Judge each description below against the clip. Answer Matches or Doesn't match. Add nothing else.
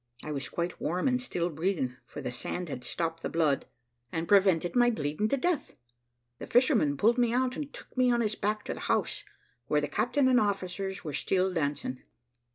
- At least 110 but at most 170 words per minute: Doesn't match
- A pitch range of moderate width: Doesn't match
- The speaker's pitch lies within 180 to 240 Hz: Matches